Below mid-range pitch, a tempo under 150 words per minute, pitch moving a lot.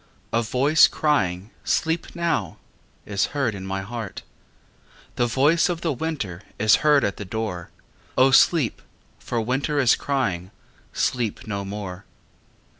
Yes: low, 120 Hz; average, 140 wpm; wide, 6.5 semitones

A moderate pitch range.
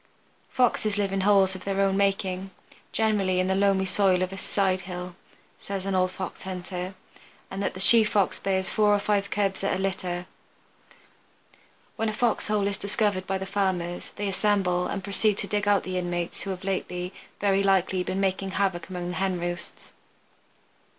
No: narrow, 1.5 semitones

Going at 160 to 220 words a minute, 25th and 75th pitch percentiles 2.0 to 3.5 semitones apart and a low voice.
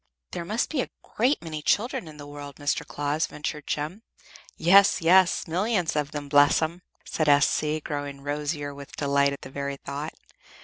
No: average, 175 wpm; average, 2.9 semitones; medium, 150 Hz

